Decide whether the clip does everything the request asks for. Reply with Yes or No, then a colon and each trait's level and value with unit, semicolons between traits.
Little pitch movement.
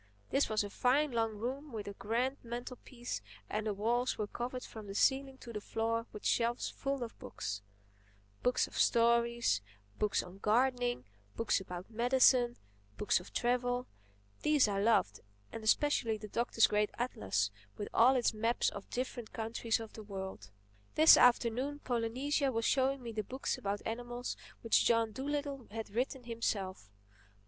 No: average, 3.0 semitones